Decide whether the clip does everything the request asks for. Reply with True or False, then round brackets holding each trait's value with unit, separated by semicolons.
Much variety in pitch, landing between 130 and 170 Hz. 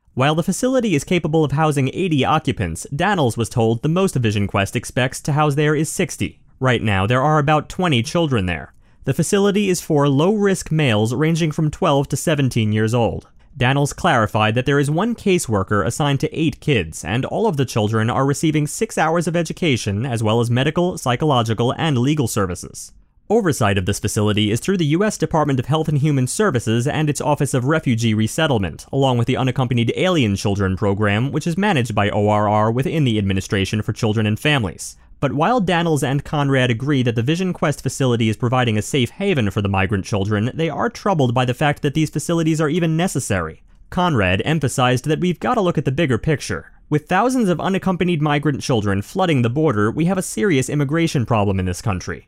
True (6.2 semitones; 140 Hz)